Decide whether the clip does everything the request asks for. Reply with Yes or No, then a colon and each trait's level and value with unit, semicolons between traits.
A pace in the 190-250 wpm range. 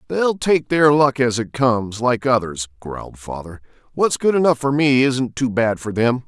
Yes: average, 200 wpm